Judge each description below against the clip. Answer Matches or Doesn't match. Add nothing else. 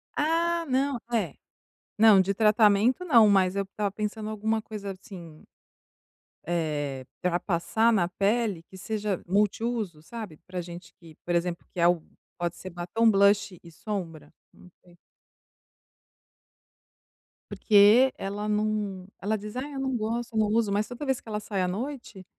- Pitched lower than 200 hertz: Doesn't match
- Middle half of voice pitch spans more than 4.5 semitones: Doesn't match